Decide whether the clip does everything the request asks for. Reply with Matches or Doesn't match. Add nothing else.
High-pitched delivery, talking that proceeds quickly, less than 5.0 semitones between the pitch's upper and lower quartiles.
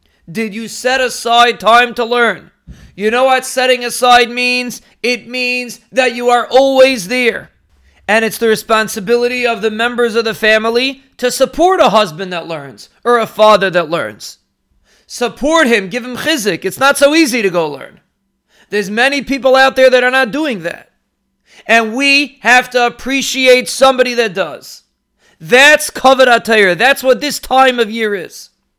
Doesn't match